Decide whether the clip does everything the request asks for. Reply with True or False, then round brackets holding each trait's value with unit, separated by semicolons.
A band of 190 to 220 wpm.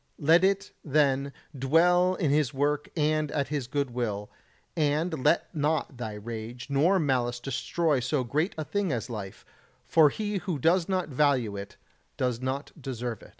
False (165 wpm)